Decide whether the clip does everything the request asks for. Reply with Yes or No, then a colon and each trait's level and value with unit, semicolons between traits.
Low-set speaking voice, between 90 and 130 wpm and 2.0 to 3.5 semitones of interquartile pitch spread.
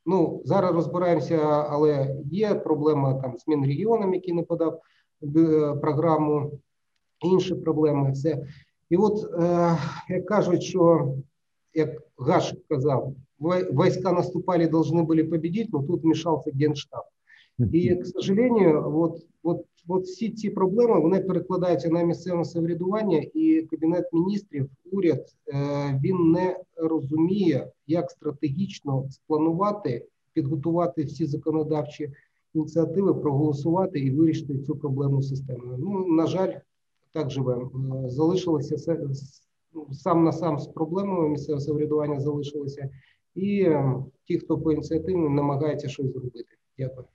No: medium, 160 Hz; average, 115 wpm; average, 2.9 semitones